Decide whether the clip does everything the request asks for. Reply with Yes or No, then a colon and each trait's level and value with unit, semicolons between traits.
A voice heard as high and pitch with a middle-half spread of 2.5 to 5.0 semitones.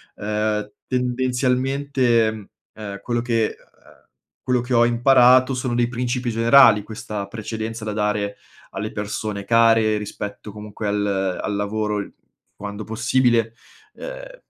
No: low, 110 Hz; average, 2.8 semitones